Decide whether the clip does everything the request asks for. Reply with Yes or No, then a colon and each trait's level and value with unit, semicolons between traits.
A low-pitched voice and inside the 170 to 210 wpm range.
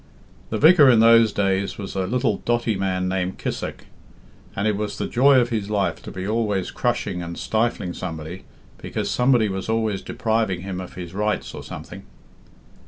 Yes: low, 105 Hz; average, 175 wpm